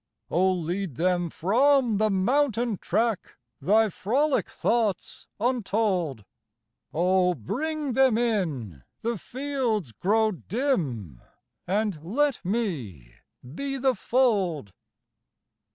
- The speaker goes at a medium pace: No, slow, 95 wpm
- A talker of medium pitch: No, high, 205 Hz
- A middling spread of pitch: No, wide, 6.2 semitones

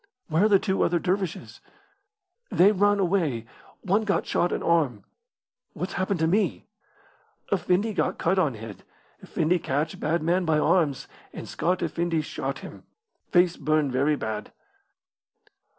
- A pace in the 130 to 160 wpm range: Yes, average, 145 wpm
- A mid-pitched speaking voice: Yes, medium, 170 Hz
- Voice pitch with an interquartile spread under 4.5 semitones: Yes, average, 3.8 semitones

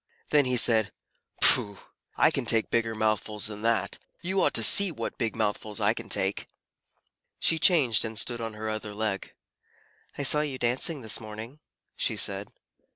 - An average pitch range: Yes, average, 3.0 semitones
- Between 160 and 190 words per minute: Yes, average, 170 wpm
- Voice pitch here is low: Yes, low, 115 Hz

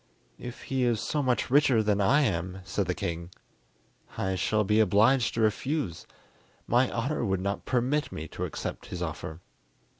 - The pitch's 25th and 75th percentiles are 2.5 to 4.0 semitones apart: No, average, 5.2 semitones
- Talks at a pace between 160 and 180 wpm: Yes, average, 170 wpm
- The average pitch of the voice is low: Yes, low, 110 Hz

